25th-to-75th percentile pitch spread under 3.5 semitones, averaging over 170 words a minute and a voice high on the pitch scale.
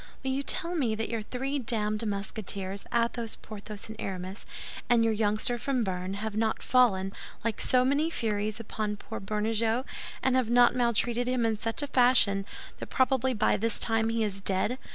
Yes: average, 2.9 semitones; average, 180 wpm; high, 225 Hz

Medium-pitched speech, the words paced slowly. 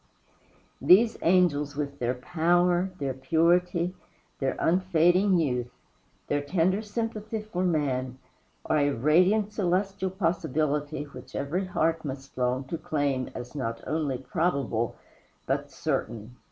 Yes: medium, 160 Hz; slow, 120 wpm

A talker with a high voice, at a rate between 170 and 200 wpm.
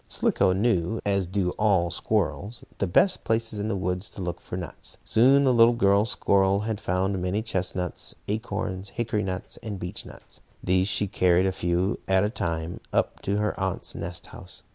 No: very low, 95 Hz; average, 185 wpm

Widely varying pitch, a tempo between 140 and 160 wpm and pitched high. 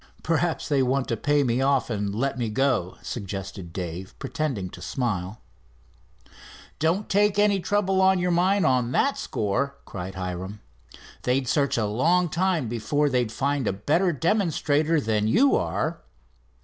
No: wide, 7.9 semitones; average, 150 wpm; low, 135 Hz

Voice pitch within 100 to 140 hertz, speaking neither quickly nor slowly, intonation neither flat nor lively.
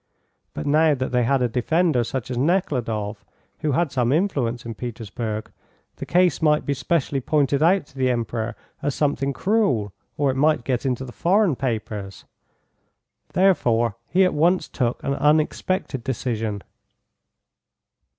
Yes: low, 135 Hz; average, 150 wpm; average, 4.8 semitones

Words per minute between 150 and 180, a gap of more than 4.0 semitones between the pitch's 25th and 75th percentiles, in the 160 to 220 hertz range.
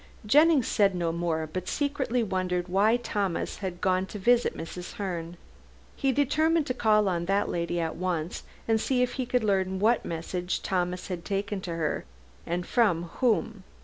Yes: average, 170 wpm; average, 4.9 semitones; high, 190 Hz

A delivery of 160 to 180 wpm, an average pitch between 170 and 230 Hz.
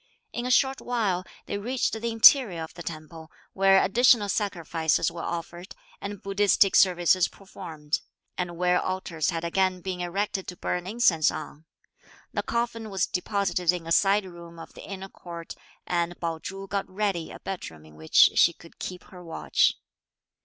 Yes: average, 170 wpm; medium, 185 Hz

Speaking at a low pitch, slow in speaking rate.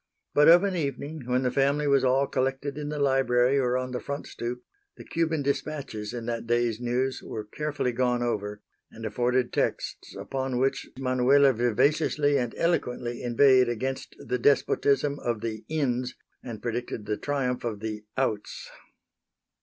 No: low, 130 Hz; average, 160 wpm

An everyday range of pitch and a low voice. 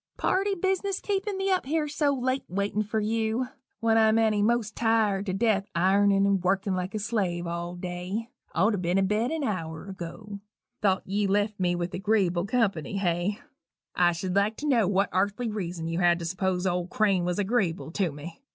No: average, 3.8 semitones; high, 200 Hz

